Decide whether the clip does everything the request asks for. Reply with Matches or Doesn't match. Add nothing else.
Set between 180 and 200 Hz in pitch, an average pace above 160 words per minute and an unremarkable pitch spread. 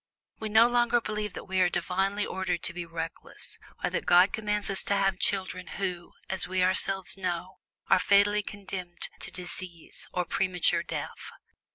Doesn't match